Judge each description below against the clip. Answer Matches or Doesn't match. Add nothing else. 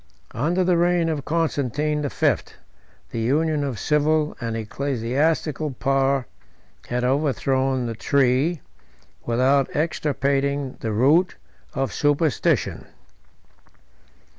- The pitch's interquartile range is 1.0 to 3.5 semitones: Matches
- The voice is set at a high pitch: Doesn't match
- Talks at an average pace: Doesn't match